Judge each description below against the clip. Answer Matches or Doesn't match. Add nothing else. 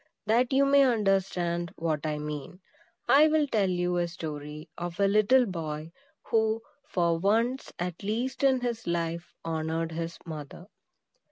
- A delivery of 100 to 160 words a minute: Matches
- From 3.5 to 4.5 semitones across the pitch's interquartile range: Doesn't match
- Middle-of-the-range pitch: Matches